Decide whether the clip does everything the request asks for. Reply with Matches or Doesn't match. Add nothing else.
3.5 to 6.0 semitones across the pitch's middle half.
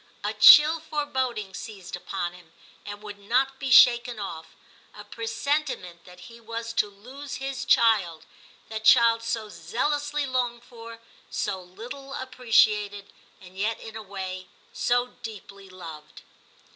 Matches